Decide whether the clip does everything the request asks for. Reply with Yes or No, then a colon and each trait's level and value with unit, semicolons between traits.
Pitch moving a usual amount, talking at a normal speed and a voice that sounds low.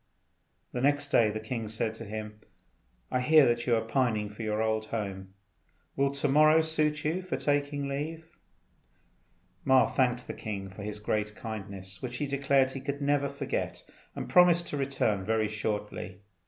Yes: average, 5.0 semitones; average, 170 wpm; low, 125 Hz